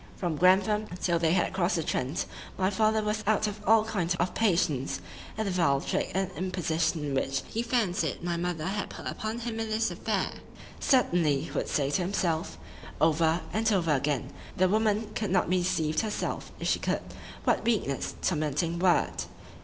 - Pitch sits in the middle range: Yes, medium, 180 Hz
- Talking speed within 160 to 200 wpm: Yes, average, 170 wpm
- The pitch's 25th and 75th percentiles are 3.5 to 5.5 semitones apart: Yes, average, 4.7 semitones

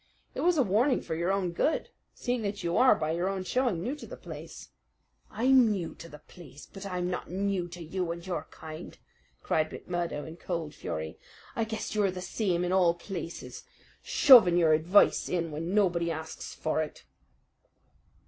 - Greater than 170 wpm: Yes, average, 185 wpm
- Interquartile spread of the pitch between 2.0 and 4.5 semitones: Yes, average, 3.3 semitones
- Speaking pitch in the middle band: Yes, medium, 180 Hz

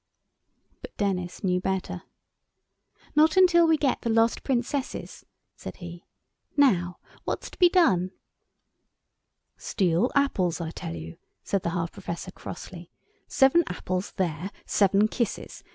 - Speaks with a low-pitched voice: No, high, 190 Hz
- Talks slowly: Yes, slow, 120 wpm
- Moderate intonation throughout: No, wide, 7.1 semitones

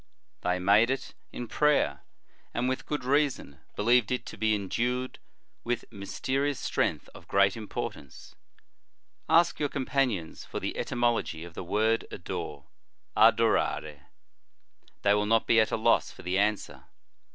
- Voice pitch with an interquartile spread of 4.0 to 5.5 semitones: Yes, average, 4.3 semitones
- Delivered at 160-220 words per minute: No, average, 140 wpm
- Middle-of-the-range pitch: No, low, 110 Hz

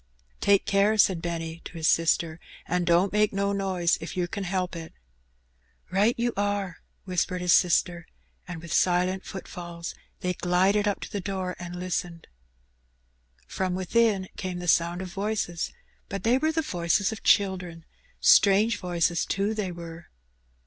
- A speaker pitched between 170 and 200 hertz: Yes, medium, 185 Hz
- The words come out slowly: No, average, 160 wpm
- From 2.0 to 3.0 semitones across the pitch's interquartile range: Yes, narrow, 2.5 semitones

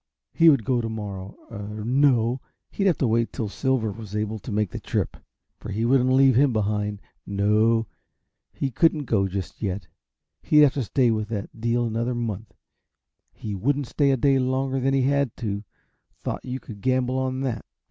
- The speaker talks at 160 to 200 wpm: Yes, average, 190 wpm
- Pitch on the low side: Yes, low, 115 Hz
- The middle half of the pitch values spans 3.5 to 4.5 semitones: Yes, average, 3.8 semitones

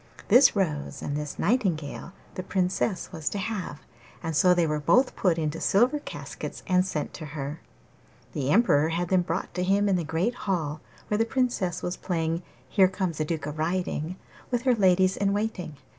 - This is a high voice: No, medium, 180 Hz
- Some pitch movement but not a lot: Yes, average, 4.1 semitones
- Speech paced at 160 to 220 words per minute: Yes, average, 190 wpm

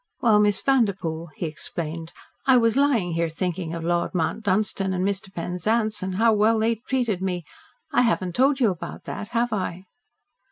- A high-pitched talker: Yes, high, 195 Hz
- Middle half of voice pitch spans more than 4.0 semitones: Yes, average, 4.5 semitones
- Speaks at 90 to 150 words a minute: No, average, 175 wpm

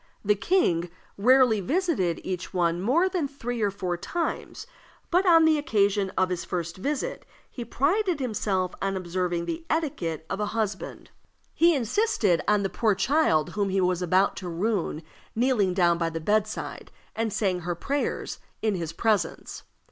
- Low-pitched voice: No, high, 200 Hz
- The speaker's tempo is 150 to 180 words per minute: Yes, average, 165 wpm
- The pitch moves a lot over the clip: Yes, wide, 6.6 semitones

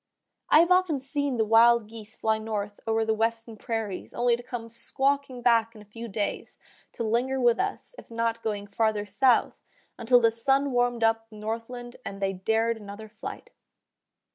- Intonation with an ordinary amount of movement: No, narrow, 1.9 semitones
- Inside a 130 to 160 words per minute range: No, average, 180 wpm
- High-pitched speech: Yes, high, 230 Hz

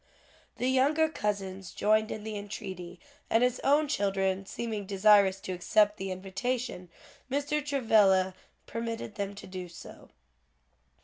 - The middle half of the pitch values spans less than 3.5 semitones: No, average, 4.2 semitones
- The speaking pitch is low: No, high, 210 Hz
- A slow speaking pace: Yes, slow, 130 wpm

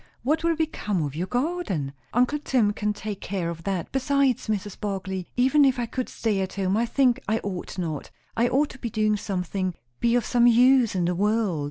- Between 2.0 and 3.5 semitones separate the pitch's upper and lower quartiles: No, average, 5.0 semitones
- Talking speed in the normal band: No, fast, 210 wpm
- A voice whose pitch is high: Yes, high, 215 Hz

